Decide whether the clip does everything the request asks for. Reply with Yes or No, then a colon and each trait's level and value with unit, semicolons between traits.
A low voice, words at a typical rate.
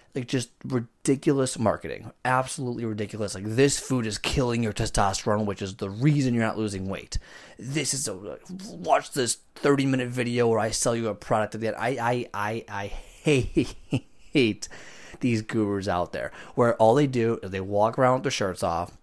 Yes: low, 115 Hz; average, 190 wpm